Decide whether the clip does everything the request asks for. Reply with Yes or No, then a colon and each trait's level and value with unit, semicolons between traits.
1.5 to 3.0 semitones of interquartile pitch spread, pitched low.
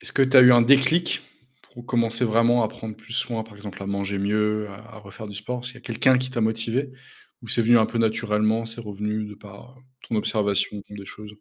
Yes: narrow, 2.5 semitones; low, 110 Hz